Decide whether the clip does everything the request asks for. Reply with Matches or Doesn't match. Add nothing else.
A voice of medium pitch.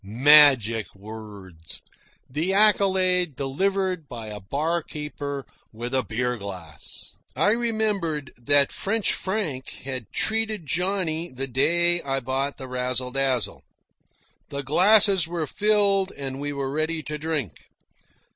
Matches